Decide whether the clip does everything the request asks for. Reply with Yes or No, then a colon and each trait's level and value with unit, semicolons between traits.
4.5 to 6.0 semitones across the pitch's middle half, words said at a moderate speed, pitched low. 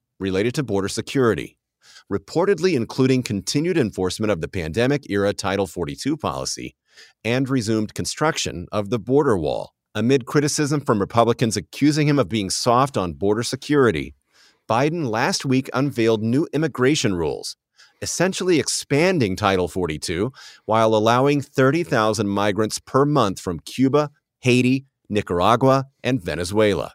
No: wide, 5.5 semitones; slow, 125 wpm; low, 120 Hz